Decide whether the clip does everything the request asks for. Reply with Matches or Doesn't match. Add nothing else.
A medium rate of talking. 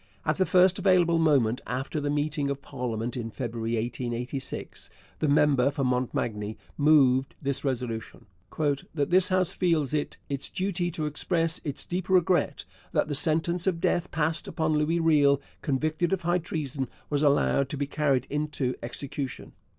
Matches